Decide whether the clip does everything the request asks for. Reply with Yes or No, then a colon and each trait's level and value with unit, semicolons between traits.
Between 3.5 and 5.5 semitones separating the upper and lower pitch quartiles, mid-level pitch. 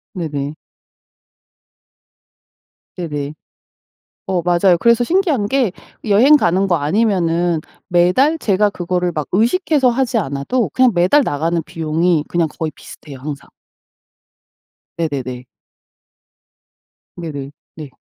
No: wide, 6.3 semitones; medium, 175 Hz